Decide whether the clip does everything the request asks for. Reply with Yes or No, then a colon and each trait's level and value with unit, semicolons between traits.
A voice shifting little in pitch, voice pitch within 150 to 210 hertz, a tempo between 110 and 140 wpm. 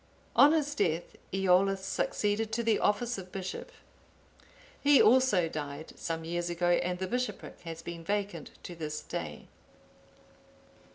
No: average, 4.6 semitones; medium, 185 Hz; slow, 135 wpm